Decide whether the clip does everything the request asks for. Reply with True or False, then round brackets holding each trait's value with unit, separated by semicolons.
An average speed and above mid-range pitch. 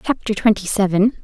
True (145 wpm; 210 Hz)